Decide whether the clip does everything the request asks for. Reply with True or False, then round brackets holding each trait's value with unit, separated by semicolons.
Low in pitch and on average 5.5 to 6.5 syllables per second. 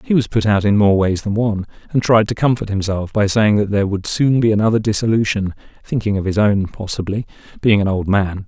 True (105 Hz; 5.9 syllables/s)